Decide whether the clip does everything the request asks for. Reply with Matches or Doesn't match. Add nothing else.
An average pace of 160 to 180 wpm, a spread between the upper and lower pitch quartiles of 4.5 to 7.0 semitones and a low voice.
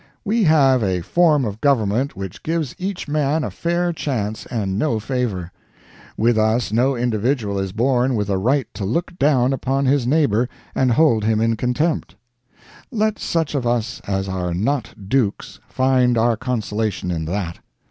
Matches